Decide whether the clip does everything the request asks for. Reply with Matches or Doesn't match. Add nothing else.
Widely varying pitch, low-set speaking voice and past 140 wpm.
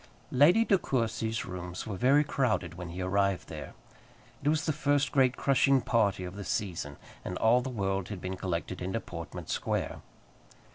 Matches